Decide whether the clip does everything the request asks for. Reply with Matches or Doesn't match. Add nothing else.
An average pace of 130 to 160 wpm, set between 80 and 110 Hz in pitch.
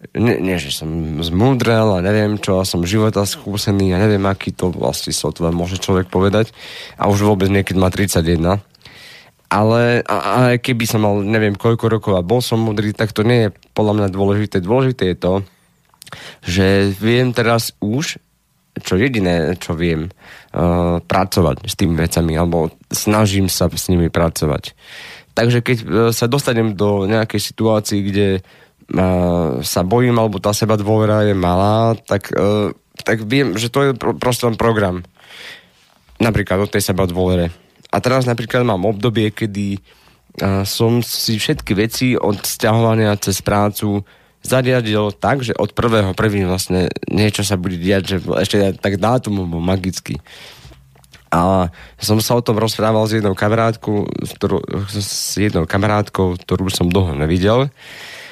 Matches